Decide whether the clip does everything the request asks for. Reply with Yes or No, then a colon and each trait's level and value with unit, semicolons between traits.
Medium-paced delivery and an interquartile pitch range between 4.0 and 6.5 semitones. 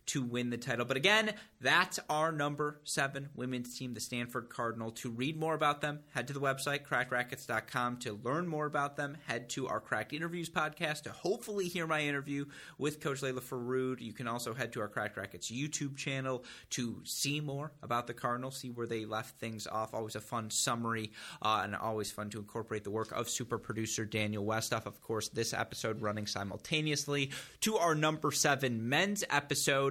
Yes: average, 195 wpm; average, 4.3 semitones